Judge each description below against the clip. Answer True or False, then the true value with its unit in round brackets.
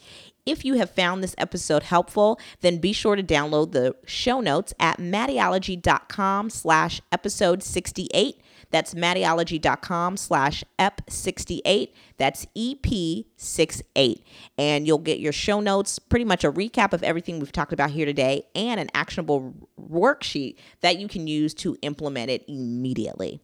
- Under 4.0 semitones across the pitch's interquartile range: False (4.7 semitones)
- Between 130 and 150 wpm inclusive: True (140 wpm)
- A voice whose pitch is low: False (175 Hz)